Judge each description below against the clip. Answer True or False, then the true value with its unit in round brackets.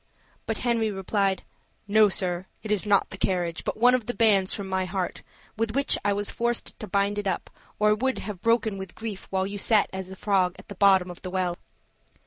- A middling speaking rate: False (225 wpm)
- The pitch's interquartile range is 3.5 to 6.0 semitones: False (2.5 semitones)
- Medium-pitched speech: False (200 Hz)